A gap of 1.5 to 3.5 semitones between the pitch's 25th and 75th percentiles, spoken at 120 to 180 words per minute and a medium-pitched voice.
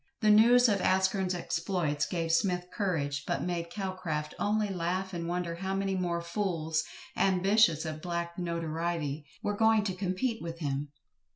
Yes: average, 2.7 semitones; average, 160 wpm; medium, 180 Hz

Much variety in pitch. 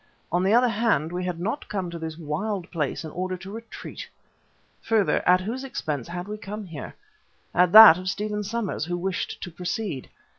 No: average, 3.7 semitones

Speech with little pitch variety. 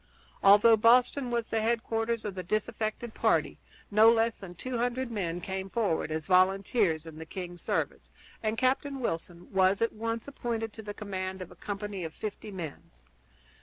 No: average, 3.6 semitones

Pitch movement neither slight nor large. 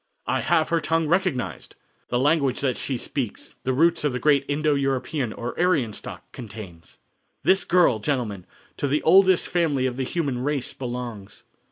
Yes: average, 4.6 semitones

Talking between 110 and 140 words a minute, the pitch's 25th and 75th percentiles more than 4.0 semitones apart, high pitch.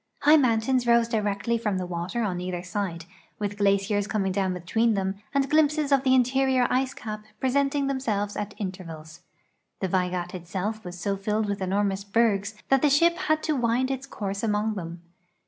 No: average, 180 wpm; average, 5.1 semitones; high, 210 Hz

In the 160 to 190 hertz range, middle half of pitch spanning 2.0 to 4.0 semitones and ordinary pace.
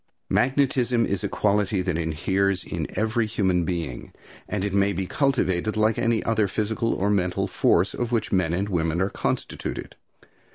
No: low, 100 Hz; average, 3.6 semitones; average, 165 wpm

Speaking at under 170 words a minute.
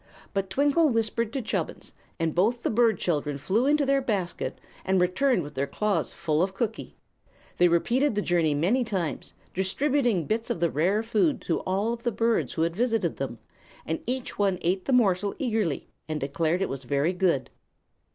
No: average, 190 wpm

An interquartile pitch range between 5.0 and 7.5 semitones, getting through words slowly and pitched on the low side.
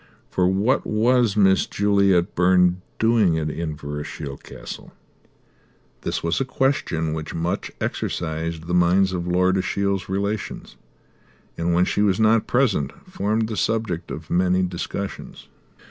No: average, 3.5 semitones; slow, 130 wpm; very low, 95 Hz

